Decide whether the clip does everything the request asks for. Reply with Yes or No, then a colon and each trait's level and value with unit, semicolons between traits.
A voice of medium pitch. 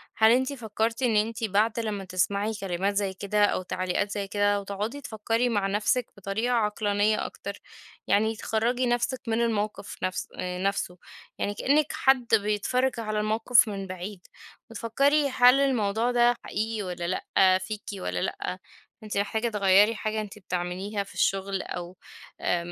No: high, 210 Hz